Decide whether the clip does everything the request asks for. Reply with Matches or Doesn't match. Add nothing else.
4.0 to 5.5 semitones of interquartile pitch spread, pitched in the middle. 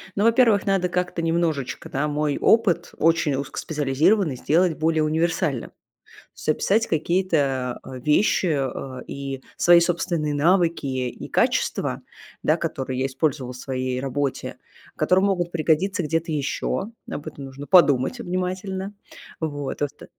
Matches